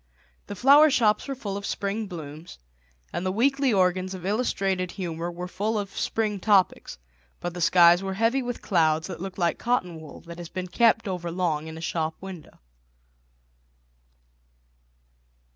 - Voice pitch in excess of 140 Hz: Yes, medium, 185 Hz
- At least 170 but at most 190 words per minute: No, average, 160 wpm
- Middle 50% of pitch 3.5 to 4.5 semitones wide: Yes, average, 3.8 semitones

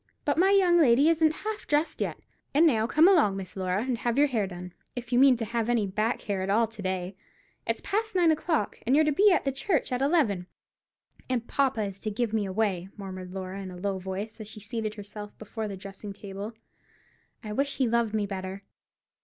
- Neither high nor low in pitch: No, high, 220 Hz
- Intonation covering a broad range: Yes, wide, 5.9 semitones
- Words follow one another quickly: Yes, fast, 220 wpm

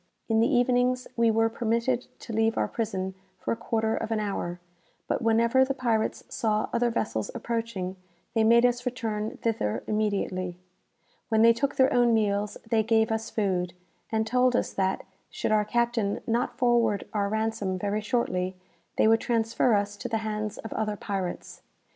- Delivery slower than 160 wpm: No, average, 170 wpm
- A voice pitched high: Yes, high, 225 Hz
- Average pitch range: No, narrow, 2.1 semitones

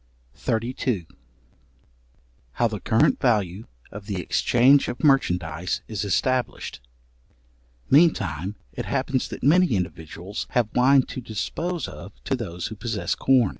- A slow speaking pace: Yes, slow, 125 wpm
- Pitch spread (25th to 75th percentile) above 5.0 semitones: Yes, wide, 5.6 semitones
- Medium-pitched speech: No, low, 115 Hz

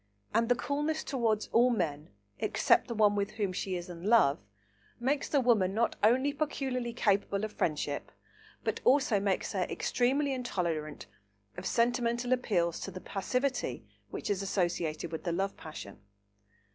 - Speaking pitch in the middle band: No, high, 210 Hz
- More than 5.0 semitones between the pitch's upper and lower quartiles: Yes, wide, 5.5 semitones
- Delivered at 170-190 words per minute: No, average, 155 wpm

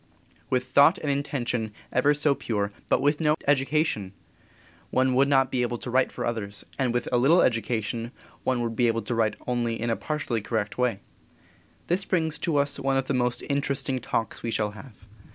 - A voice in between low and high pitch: No, low, 125 Hz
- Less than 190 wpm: No, average, 195 wpm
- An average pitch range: Yes, average, 3.4 semitones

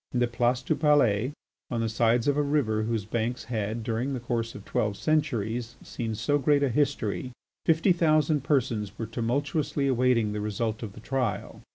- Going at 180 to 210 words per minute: Yes, average, 185 wpm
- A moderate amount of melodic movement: Yes, average, 4.2 semitones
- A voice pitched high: No, low, 120 Hz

